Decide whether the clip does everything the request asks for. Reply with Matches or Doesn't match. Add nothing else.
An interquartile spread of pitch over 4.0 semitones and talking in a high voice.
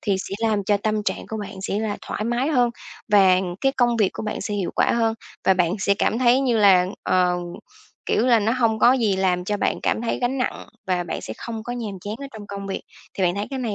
Doesn't match